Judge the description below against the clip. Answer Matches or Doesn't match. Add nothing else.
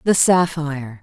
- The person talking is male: Doesn't match